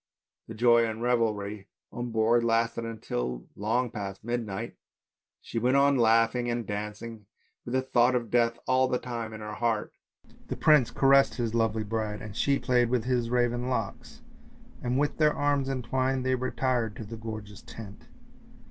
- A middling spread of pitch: No, narrow, 2.3 semitones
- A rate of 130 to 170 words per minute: Yes, average, 165 wpm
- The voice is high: No, low, 115 Hz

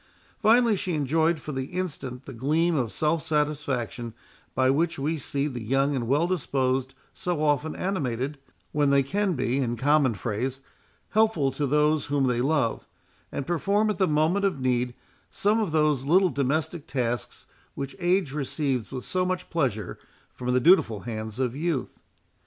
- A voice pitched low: No, medium, 145 Hz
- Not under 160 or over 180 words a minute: Yes, average, 165 wpm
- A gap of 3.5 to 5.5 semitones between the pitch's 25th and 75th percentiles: Yes, average, 4.3 semitones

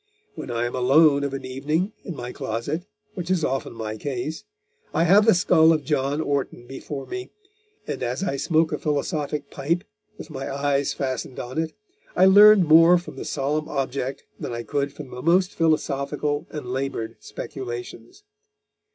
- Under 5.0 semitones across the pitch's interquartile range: Yes, average, 3.6 semitones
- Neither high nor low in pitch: Yes, medium, 145 Hz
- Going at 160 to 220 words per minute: Yes, average, 170 wpm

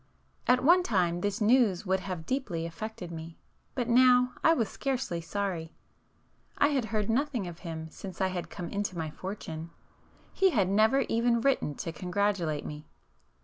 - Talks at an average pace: Yes, average, 160 wpm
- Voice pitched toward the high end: Yes, high, 200 Hz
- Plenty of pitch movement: Yes, wide, 6.3 semitones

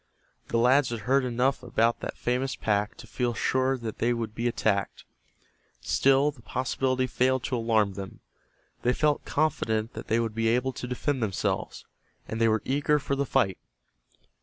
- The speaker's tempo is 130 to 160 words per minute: No, average, 175 wpm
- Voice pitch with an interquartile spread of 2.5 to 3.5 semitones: Yes, average, 2.8 semitones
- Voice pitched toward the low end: Yes, low, 120 Hz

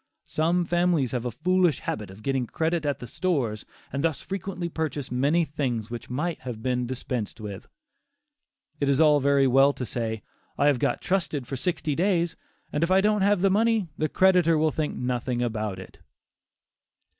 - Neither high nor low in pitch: Yes, medium, 145 Hz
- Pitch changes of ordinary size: No, wide, 5.8 semitones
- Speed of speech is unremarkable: Yes, average, 180 wpm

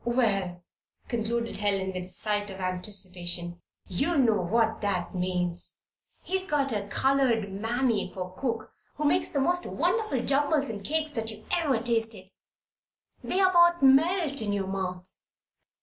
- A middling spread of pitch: No, wide, 6.4 semitones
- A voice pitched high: Yes, high, 225 Hz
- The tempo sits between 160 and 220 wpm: No, average, 150 wpm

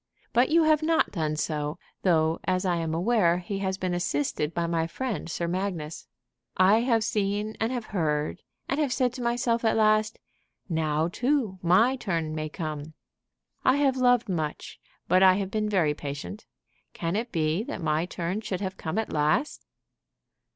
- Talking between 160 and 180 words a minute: Yes, average, 175 wpm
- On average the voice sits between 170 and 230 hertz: Yes, medium, 185 Hz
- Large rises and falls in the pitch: Yes, wide, 5.7 semitones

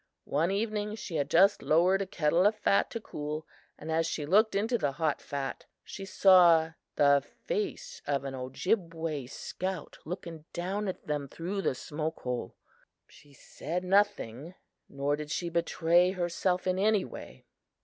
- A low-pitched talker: No, medium, 170 Hz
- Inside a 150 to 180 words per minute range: Yes, average, 160 wpm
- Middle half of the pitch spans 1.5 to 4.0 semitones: No, average, 4.5 semitones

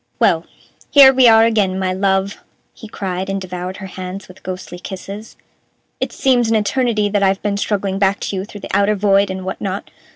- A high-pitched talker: Yes, high, 195 Hz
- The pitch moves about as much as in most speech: No, narrow, 1.9 semitones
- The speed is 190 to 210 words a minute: Yes, average, 200 wpm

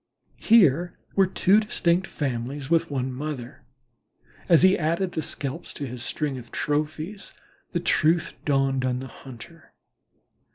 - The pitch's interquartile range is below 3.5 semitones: No, average, 4.6 semitones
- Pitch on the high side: No, medium, 150 Hz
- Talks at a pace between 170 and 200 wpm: No, average, 140 wpm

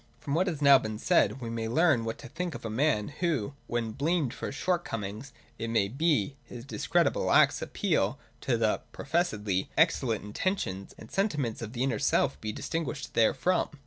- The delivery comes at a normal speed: Yes, average, 185 wpm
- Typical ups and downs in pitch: No, wide, 6.1 semitones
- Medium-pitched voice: No, low, 125 Hz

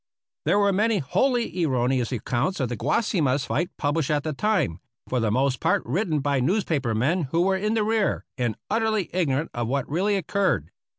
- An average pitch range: No, wide, 7.4 semitones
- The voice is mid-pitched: Yes, medium, 155 Hz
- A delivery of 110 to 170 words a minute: No, average, 185 wpm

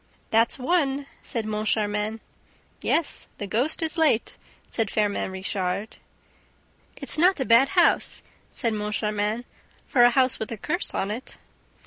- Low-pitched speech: No, high, 225 Hz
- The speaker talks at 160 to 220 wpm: No, slow, 135 wpm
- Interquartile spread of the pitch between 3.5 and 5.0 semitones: Yes, average, 4.2 semitones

